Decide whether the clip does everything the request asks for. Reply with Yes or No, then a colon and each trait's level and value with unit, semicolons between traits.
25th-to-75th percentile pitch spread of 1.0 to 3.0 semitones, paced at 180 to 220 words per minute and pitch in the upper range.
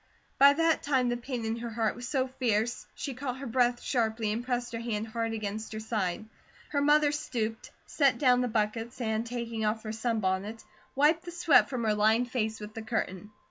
Yes: average, 2.7 semitones; fast, 205 wpm; high, 235 Hz